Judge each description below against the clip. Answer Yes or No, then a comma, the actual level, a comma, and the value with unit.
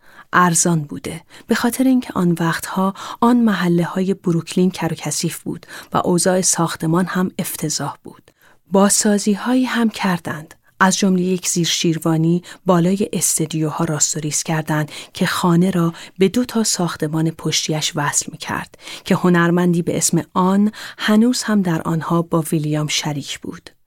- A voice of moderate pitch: Yes, medium, 175 Hz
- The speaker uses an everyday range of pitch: Yes, average, 3.0 semitones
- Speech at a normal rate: Yes, average, 140 wpm